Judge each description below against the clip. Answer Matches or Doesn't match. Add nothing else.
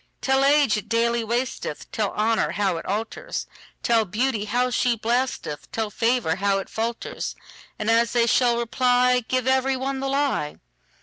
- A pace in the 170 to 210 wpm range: Doesn't match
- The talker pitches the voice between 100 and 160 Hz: Doesn't match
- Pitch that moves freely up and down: Doesn't match